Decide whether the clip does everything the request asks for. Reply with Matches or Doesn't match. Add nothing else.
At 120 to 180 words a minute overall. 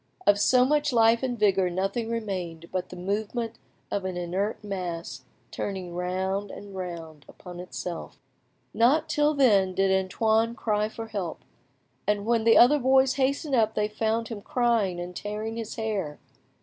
Matches